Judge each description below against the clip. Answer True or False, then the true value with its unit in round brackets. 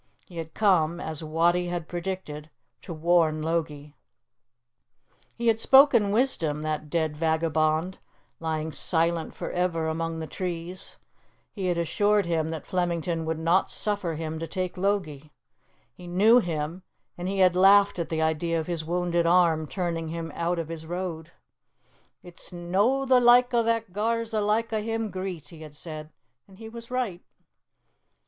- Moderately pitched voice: True (175 Hz)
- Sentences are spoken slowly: False (165 wpm)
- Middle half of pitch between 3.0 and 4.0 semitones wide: True (3.4 semitones)